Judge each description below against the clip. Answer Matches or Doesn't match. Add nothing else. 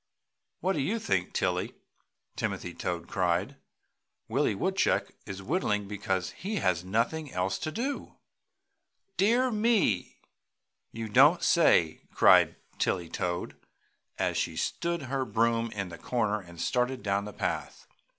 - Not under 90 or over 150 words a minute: Matches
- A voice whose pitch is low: Matches